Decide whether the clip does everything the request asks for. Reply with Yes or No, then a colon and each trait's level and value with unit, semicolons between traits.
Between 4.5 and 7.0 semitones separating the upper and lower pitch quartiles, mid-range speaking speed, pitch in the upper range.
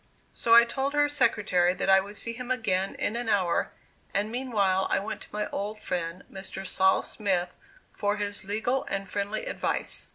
No: average, 3.3 semitones; average, 185 wpm; high, 205 Hz